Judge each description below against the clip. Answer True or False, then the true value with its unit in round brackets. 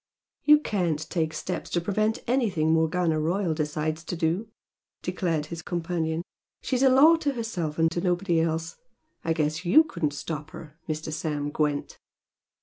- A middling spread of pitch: True (3.2 semitones)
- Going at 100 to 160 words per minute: True (155 wpm)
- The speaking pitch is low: False (165 Hz)